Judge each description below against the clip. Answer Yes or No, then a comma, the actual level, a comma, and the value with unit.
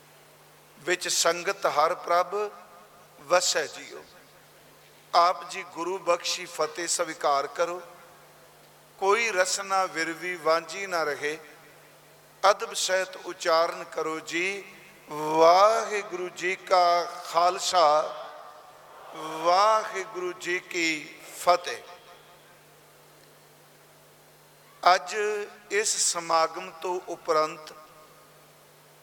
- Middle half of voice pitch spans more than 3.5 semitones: No, narrow, 2.5 semitones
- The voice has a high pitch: No, medium, 175 Hz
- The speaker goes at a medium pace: No, slow, 80 wpm